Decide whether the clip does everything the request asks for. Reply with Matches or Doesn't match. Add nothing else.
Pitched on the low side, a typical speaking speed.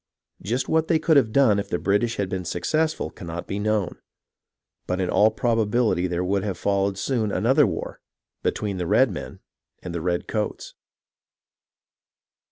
Matches